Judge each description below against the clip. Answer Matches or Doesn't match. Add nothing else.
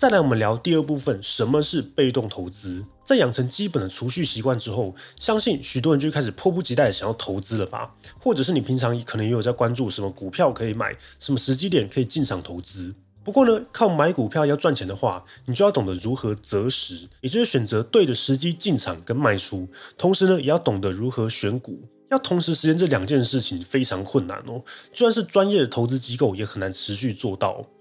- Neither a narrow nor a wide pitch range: Doesn't match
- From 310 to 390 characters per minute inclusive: Matches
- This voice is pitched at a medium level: Doesn't match